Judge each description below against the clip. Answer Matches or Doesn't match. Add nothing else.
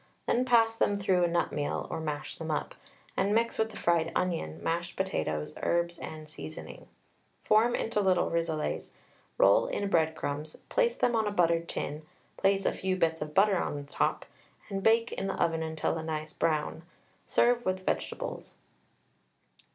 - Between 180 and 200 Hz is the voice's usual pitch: Doesn't match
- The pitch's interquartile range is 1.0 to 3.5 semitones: Doesn't match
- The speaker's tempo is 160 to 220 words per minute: Matches